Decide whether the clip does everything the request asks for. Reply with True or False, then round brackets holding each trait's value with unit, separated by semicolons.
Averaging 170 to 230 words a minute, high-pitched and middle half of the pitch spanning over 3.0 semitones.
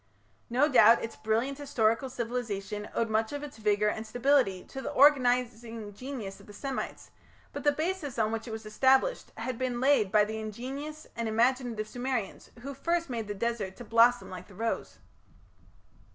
True (175 wpm; 235 Hz; 3.5 semitones)